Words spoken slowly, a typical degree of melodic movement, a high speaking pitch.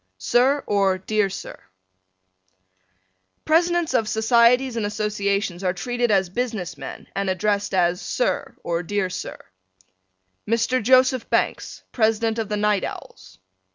Yes: slow, 125 wpm; average, 4.0 semitones; high, 210 Hz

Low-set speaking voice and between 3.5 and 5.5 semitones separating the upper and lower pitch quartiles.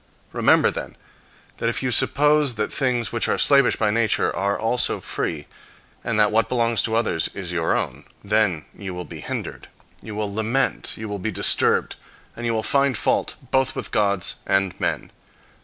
No: low, 110 Hz; average, 3.1 semitones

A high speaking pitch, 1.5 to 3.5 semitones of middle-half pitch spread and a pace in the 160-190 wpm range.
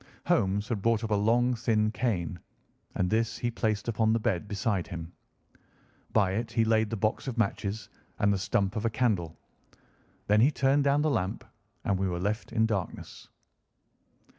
No: low, 110 Hz; average, 2.8 semitones; average, 180 wpm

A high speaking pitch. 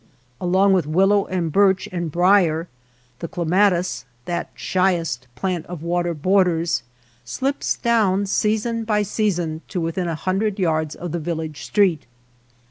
No: medium, 180 Hz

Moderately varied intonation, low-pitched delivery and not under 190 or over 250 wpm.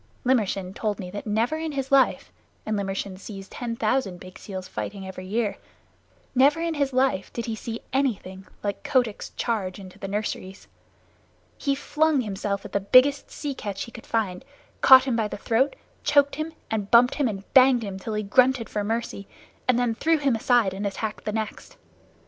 No: average, 4.8 semitones; high, 225 Hz; average, 195 wpm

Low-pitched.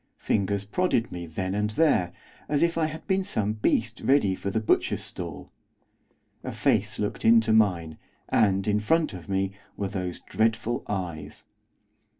Yes: low, 105 Hz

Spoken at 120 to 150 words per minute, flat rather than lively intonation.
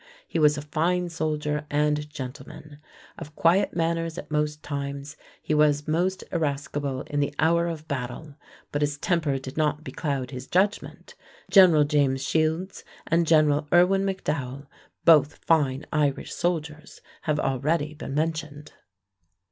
Yes: average, 140 wpm; narrow, 2.2 semitones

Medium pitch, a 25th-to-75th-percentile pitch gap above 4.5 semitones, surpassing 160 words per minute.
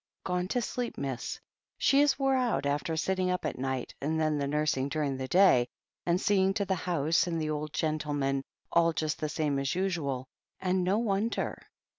Yes: medium, 160 Hz; average, 4.9 semitones; average, 195 wpm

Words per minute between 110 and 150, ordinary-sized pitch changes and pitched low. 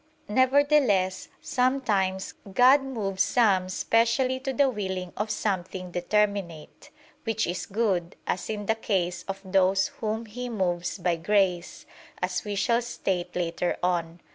No: average, 140 wpm; average, 4.2 semitones; high, 195 Hz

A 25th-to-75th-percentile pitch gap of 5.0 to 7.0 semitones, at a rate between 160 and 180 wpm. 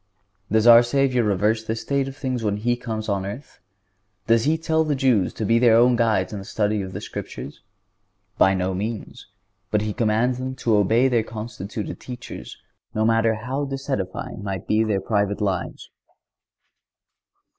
No: average, 3.3 semitones; average, 170 wpm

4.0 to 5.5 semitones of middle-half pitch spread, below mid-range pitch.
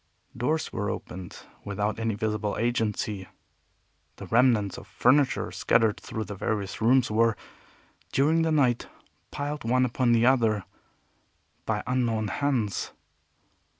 No: average, 3.3 semitones; low, 115 Hz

